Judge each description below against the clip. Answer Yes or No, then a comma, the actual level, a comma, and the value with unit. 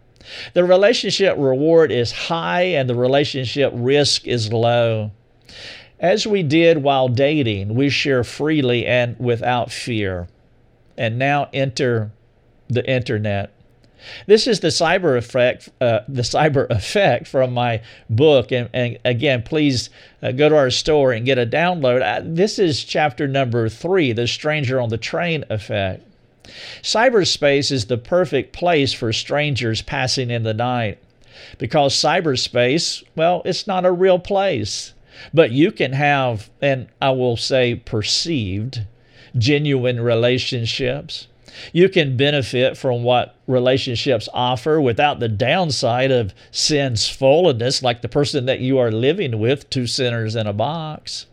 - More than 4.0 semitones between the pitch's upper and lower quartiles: No, average, 3.5 semitones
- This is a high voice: No, low, 130 Hz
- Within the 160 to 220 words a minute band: No, average, 140 wpm